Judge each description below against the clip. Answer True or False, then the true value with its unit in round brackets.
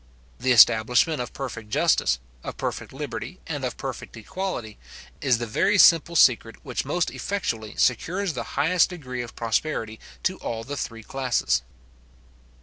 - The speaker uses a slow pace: False (145 wpm)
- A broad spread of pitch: True (6.4 semitones)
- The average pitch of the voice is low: True (125 Hz)